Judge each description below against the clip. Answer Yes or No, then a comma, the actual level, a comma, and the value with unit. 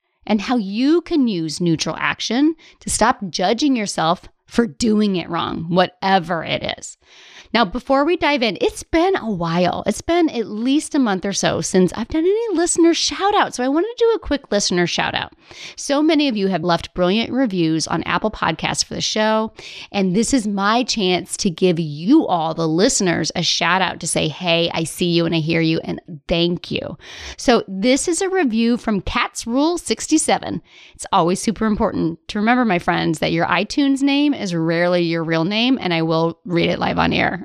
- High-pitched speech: Yes, high, 210 Hz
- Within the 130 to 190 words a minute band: No, fast, 205 wpm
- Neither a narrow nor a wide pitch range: No, wide, 7.8 semitones